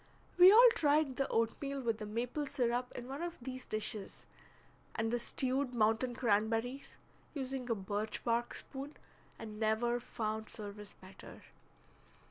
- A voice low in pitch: No, high, 240 Hz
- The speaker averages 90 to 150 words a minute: Yes, average, 140 wpm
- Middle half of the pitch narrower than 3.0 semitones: No, average, 3.4 semitones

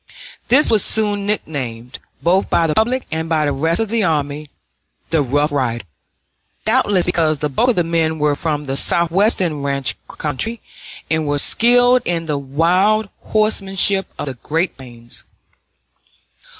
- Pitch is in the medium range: Yes, medium, 165 Hz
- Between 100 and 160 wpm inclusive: Yes, average, 150 wpm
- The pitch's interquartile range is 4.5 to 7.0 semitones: Yes, wide, 5.6 semitones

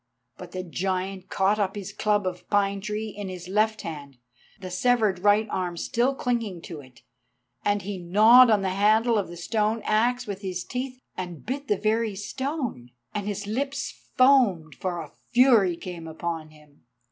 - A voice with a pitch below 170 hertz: No, high, 200 Hz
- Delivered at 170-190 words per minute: Yes, average, 175 wpm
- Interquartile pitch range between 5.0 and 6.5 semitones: No, average, 3.7 semitones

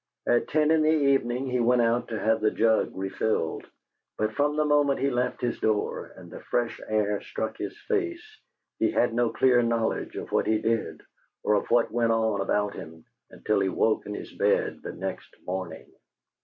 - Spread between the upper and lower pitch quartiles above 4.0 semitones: No, average, 3.6 semitones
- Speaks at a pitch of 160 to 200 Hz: No, low, 115 Hz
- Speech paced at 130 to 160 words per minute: No, average, 195 wpm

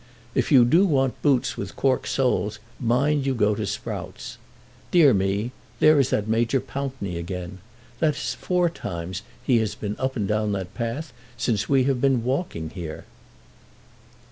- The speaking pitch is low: Yes, low, 120 Hz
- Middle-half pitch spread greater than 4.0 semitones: Yes, average, 5.2 semitones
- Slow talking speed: No, average, 165 wpm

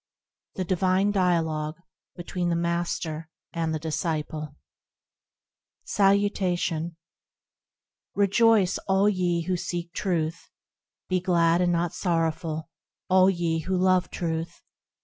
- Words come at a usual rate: No, slow, 105 wpm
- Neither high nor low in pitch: Yes, medium, 175 Hz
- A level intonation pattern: Yes, narrow, 2.3 semitones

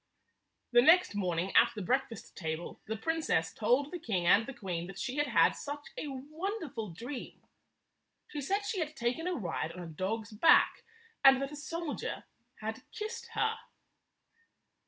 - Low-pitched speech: No, very high, 255 Hz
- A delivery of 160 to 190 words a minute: Yes, average, 165 wpm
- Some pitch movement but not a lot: No, wide, 8.0 semitones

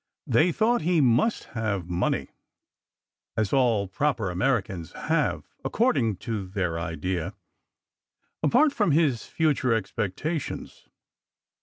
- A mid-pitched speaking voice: No, low, 115 Hz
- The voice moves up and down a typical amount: No, wide, 8.6 semitones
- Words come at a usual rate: No, slow, 110 wpm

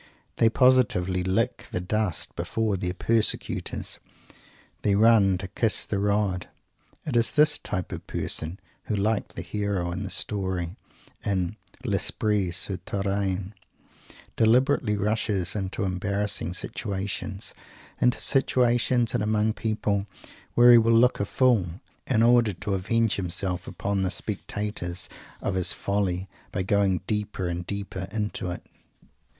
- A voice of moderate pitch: No, low, 100 Hz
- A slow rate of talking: Yes, slow, 130 wpm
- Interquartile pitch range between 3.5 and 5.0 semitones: No, average, 3.1 semitones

